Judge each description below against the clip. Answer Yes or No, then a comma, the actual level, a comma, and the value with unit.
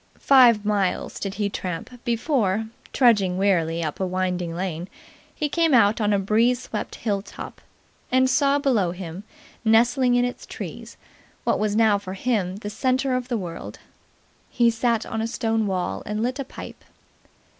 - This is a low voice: No, high, 215 Hz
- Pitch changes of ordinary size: Yes, average, 4.5 semitones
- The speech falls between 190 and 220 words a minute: No, average, 165 wpm